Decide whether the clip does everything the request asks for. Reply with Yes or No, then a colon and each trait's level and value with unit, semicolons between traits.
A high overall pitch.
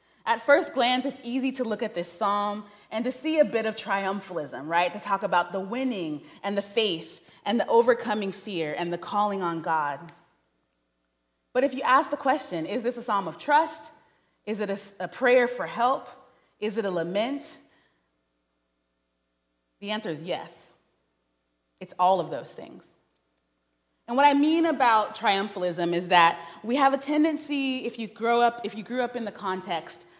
Yes: high, 205 Hz